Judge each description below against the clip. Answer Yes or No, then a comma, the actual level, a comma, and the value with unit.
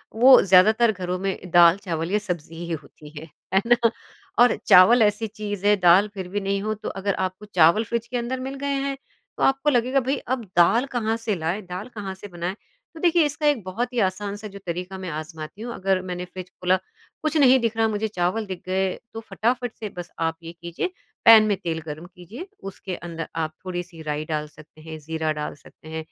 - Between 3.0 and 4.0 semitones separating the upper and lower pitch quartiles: No, average, 4.5 semitones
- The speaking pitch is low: No, high, 190 Hz